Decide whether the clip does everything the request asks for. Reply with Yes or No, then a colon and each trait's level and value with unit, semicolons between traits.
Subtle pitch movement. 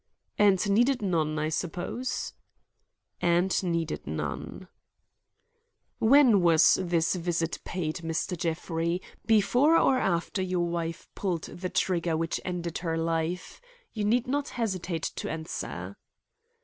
No: average, 3.4 semitones